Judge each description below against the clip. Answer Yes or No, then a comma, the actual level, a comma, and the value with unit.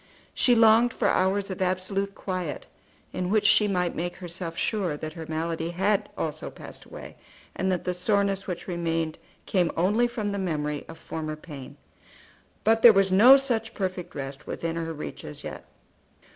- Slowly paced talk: No, average, 170 wpm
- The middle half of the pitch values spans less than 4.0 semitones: Yes, average, 3.6 semitones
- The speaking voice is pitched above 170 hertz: Yes, medium, 185 Hz